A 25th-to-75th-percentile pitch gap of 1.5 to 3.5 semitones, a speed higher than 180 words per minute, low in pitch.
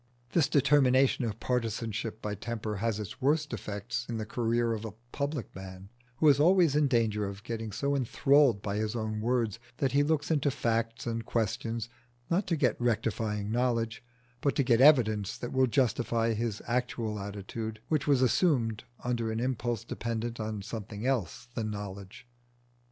No: average, 3.2 semitones; average, 170 wpm; low, 115 Hz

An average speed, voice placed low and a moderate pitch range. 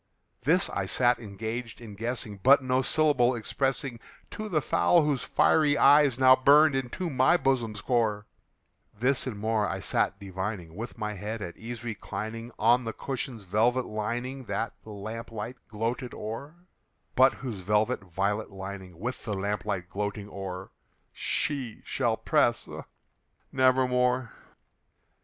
Yes: average, 145 wpm; low, 115 Hz; average, 3.8 semitones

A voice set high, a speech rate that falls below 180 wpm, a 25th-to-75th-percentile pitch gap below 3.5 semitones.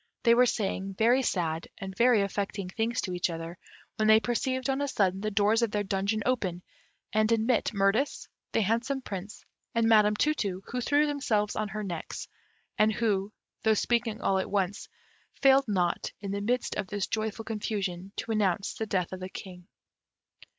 No: high, 210 Hz; average, 185 wpm; average, 3.1 semitones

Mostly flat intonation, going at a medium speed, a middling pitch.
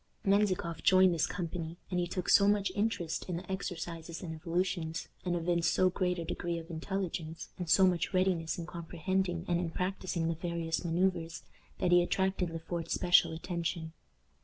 Yes: narrow, 2.0 semitones; average, 175 wpm; medium, 175 Hz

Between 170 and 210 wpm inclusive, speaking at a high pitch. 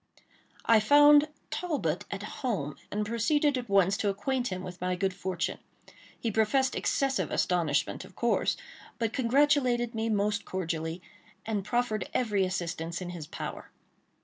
No: average, 145 wpm; high, 210 Hz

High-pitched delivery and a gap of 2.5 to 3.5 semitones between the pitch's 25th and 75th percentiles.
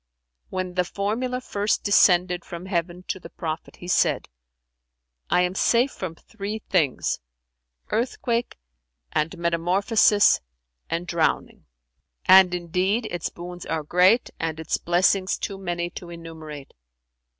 No: medium, 180 Hz; average, 2.8 semitones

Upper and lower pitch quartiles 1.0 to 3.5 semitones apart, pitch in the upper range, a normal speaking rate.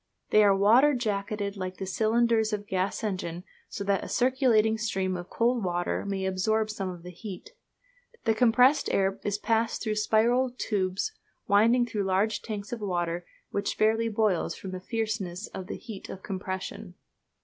Yes: average, 2.9 semitones; high, 210 Hz; average, 170 wpm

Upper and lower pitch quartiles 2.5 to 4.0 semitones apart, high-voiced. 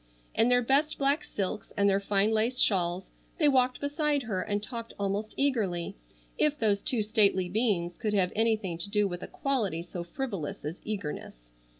No: average, 4.8 semitones; high, 210 Hz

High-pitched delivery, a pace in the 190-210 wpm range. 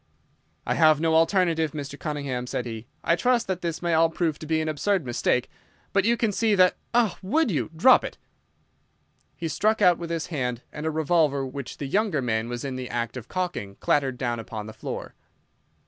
No: medium, 155 Hz; average, 200 wpm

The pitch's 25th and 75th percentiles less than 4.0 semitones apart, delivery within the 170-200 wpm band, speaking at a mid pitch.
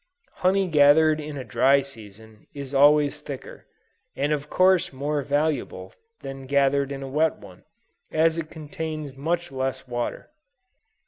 No: narrow, 2.5 semitones; average, 145 wpm; medium, 145 Hz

